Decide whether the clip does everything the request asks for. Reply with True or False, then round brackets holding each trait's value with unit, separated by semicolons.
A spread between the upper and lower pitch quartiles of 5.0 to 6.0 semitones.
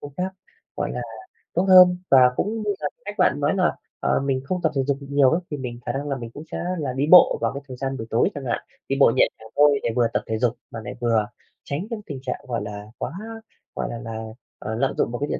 False (3.8 semitones)